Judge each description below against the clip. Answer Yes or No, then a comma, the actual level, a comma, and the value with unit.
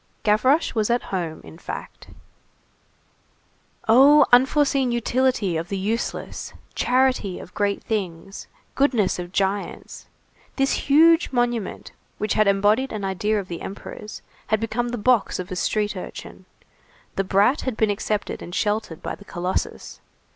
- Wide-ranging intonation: No, average, 4.2 semitones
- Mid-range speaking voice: No, high, 215 Hz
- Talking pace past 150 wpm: No, average, 140 wpm